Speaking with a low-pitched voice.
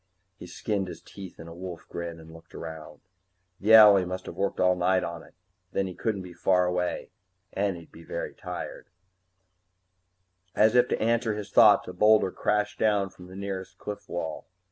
Yes: very low, 95 Hz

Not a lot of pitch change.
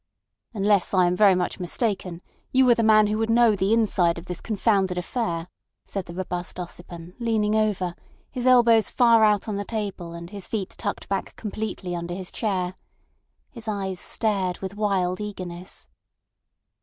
No: average, 3.3 semitones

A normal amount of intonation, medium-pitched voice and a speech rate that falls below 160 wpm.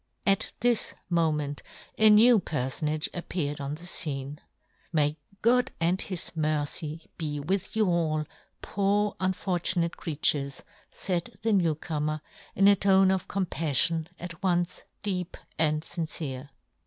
Yes: average, 3.8 semitones; medium, 170 Hz; average, 150 wpm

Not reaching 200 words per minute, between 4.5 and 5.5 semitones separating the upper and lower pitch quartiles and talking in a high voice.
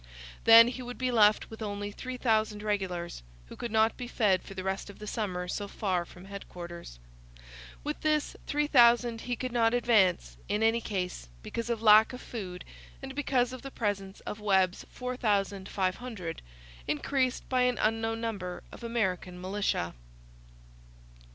No: average, 155 wpm; average, 4.0 semitones; high, 215 Hz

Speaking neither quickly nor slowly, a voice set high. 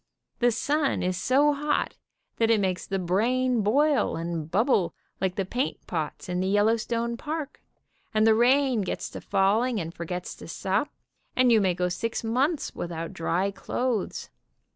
Yes: average, 165 wpm; high, 220 Hz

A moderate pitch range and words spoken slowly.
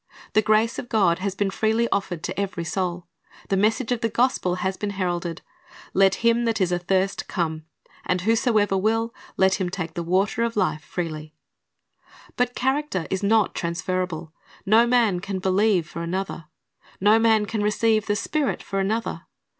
No: average, 3.6 semitones; average, 170 wpm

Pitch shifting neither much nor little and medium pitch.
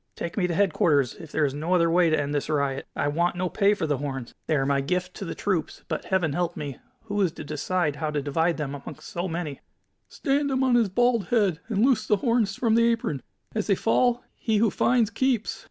No: wide, 6.7 semitones; medium, 180 Hz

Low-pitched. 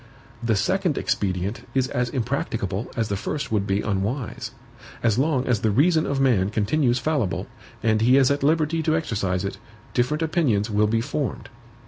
Yes: low, 120 Hz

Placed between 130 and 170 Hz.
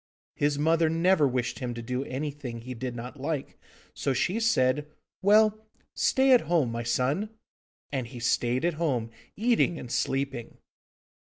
Yes: medium, 140 Hz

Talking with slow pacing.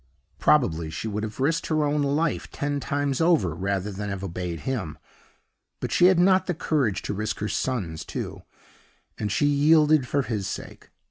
No: average, 180 wpm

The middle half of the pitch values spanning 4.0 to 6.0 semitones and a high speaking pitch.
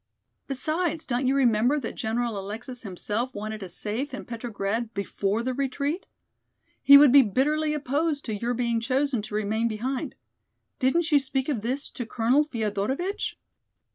Yes: average, 4.3 semitones; very high, 250 Hz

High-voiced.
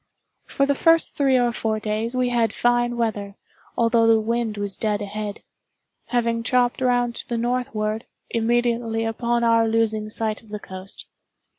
Yes: high, 230 Hz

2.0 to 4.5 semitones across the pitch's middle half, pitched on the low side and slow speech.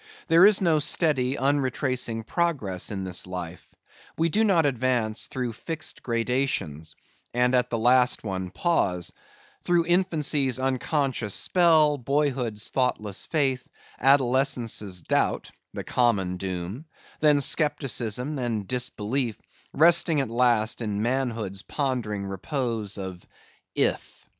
No: wide, 5.4 semitones; low, 125 Hz; slow, 115 wpm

